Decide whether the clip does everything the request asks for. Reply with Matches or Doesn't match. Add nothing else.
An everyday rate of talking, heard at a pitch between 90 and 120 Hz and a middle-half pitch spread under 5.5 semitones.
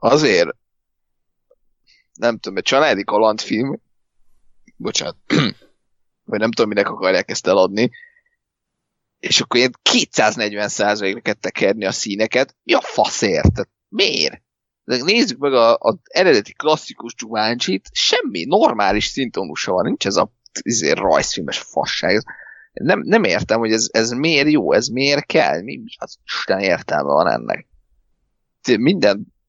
Doesn't match